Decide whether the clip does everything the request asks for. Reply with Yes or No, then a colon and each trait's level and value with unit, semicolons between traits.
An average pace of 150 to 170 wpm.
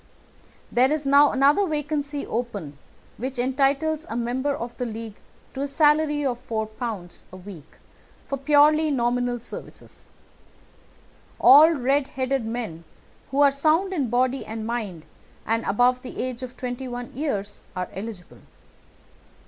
No: average, 140 wpm